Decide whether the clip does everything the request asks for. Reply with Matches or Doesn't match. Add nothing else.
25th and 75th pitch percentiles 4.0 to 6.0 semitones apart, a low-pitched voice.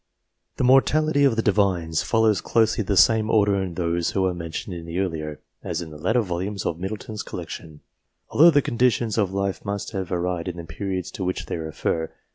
Matches